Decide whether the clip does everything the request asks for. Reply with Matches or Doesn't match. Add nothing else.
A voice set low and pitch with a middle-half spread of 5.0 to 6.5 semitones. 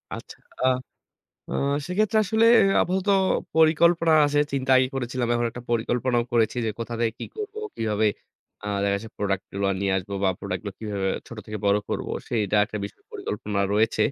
Matches